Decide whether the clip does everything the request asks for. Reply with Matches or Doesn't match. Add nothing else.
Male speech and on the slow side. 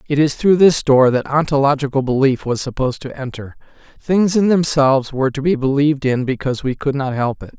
Doesn't match